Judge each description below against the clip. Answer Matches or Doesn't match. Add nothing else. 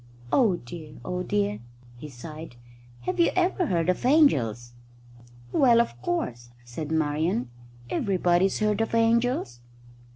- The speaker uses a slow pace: Matches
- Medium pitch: Matches